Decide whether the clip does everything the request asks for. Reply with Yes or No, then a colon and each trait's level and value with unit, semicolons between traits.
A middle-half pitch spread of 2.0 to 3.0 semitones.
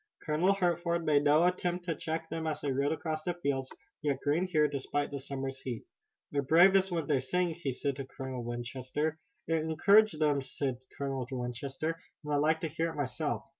No: average, 3.4 semitones